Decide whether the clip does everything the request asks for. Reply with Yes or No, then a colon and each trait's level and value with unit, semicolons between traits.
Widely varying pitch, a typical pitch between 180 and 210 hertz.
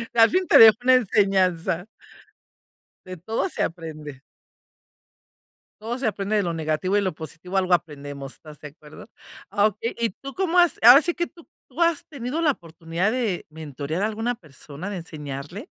Yes: wide, 6.7 semitones; high, 190 Hz